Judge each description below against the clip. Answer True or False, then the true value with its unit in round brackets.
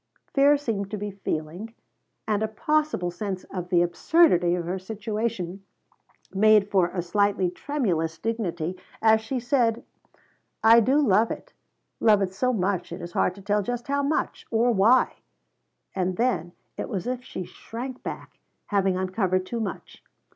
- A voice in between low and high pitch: False (205 Hz)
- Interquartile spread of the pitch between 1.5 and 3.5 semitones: False (4.2 semitones)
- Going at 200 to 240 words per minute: False (160 wpm)